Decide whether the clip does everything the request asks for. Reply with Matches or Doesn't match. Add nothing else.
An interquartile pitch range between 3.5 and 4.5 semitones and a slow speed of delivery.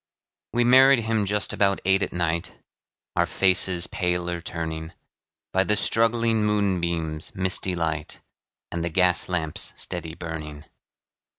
Matches